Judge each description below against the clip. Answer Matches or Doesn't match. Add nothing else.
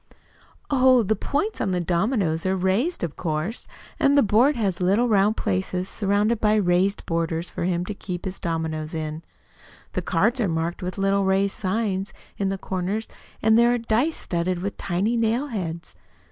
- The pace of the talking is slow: Doesn't match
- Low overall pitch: Doesn't match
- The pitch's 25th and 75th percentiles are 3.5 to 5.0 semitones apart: Matches